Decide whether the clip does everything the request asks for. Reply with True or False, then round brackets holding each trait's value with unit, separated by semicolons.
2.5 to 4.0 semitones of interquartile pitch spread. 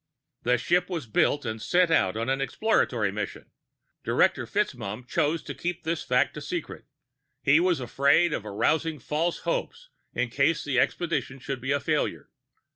False (5.4 semitones)